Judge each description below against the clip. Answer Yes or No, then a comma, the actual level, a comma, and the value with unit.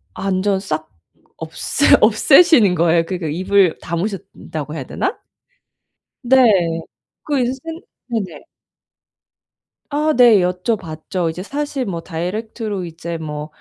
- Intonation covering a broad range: Yes, wide, 6.2 semitones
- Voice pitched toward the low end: No, high, 190 Hz